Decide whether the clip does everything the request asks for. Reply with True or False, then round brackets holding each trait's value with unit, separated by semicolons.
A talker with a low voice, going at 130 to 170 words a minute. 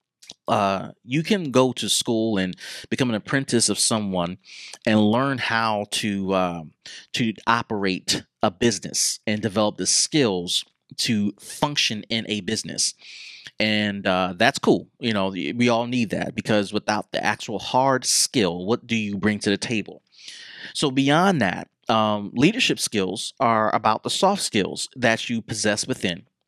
True (110 Hz; 155 wpm)